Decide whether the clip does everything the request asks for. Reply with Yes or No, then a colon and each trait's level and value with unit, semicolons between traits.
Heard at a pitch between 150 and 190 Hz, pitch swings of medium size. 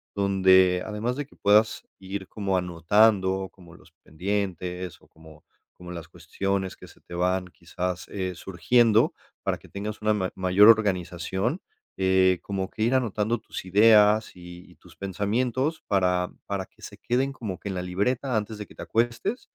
No: very low, 95 Hz; average, 3.0 semitones